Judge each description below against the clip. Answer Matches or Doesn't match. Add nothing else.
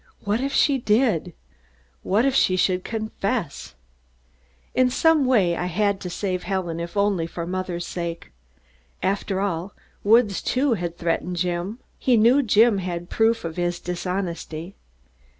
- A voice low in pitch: Doesn't match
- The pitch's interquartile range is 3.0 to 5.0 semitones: Matches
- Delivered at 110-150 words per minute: Matches